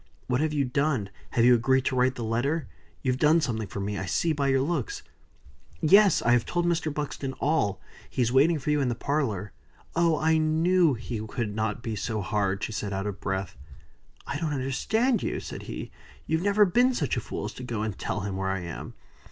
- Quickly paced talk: Yes, fast, 220 wpm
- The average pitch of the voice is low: Yes, low, 130 Hz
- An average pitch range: No, wide, 6.5 semitones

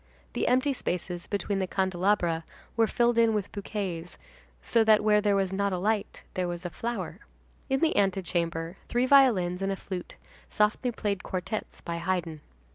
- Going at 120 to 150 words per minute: No, average, 170 wpm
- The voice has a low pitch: No, high, 195 Hz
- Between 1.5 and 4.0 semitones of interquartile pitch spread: Yes, average, 3.7 semitones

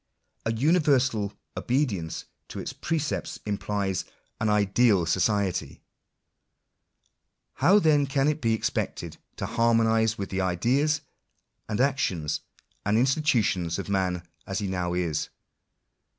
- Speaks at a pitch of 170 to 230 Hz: No, low, 110 Hz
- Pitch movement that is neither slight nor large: No, wide, 6.0 semitones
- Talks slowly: Yes, slow, 120 wpm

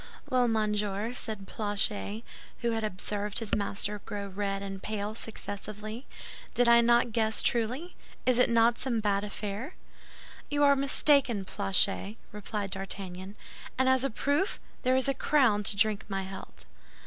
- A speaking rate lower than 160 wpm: Yes, average, 150 wpm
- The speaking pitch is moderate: No, high, 215 Hz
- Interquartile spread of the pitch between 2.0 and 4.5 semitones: Yes, average, 3.2 semitones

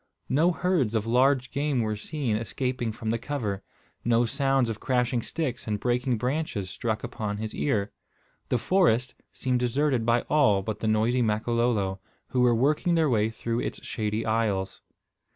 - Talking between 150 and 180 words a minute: Yes, average, 165 wpm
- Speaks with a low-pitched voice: Yes, low, 120 Hz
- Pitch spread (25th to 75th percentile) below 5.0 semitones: Yes, average, 3.3 semitones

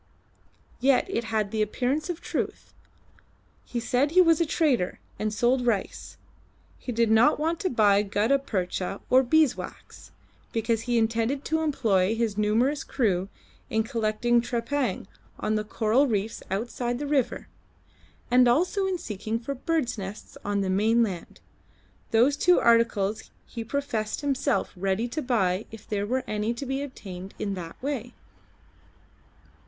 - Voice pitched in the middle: No, high, 230 Hz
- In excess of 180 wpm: No, average, 150 wpm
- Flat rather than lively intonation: No, average, 4.4 semitones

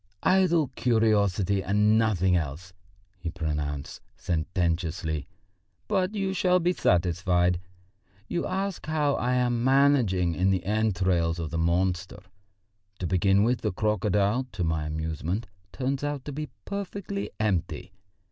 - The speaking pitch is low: Yes, low, 100 Hz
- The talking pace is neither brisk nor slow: No, slow, 130 wpm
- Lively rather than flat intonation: Yes, wide, 7.3 semitones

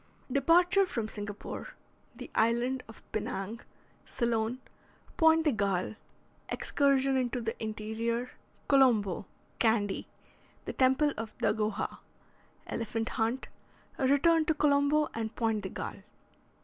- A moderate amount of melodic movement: Yes, average, 4.1 semitones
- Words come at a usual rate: No, slow, 110 wpm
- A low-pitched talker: No, high, 235 Hz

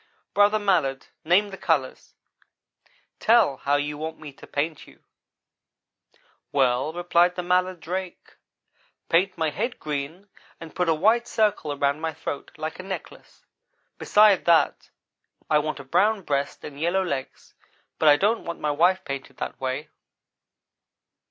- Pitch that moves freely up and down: No, average, 4.5 semitones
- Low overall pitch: No, medium, 160 Hz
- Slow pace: No, average, 145 wpm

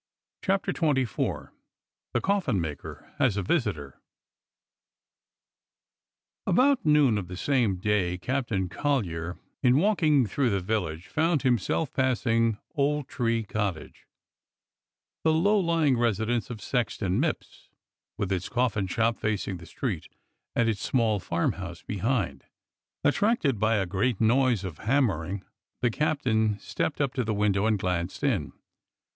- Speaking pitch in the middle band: No, low, 115 Hz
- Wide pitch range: Yes, wide, 6.0 semitones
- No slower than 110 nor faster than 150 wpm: Yes, average, 140 wpm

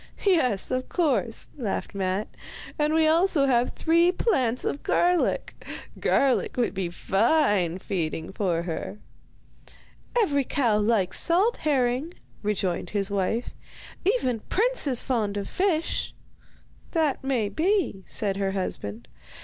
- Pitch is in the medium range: No, high, 245 Hz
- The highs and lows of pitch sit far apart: Yes, wide, 8.3 semitones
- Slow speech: Yes, slow, 125 wpm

